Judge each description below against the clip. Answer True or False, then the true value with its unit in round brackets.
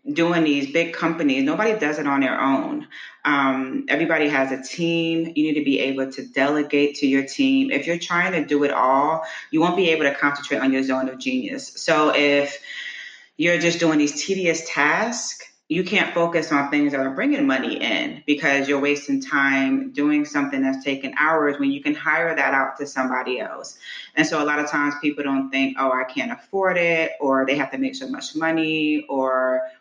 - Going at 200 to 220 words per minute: True (205 wpm)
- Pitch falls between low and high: True (150 Hz)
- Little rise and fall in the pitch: False (3.8 semitones)